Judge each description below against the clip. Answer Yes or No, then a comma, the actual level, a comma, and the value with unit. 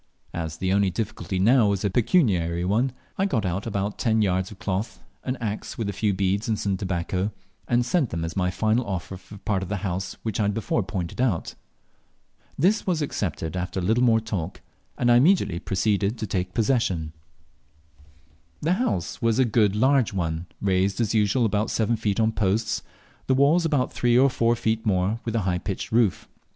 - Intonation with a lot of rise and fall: No, average, 3.9 semitones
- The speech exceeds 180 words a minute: Yes, average, 200 wpm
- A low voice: Yes, low, 105 Hz